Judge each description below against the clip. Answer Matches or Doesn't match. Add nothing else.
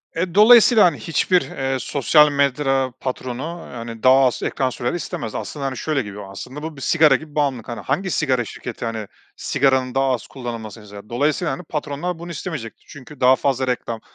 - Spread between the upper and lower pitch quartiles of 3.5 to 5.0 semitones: Matches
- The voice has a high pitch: Doesn't match